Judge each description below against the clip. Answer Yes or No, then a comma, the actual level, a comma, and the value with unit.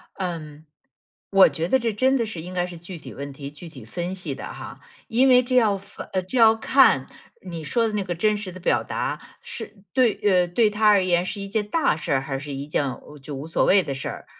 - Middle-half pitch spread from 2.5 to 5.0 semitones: No, wide, 5.6 semitones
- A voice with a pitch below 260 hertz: Yes, medium, 185 Hz